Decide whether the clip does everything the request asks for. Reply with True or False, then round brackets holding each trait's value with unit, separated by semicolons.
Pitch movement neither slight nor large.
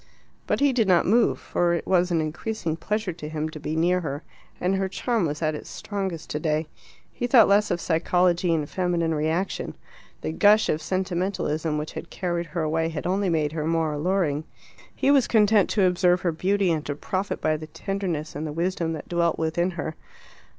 True (3.4 semitones)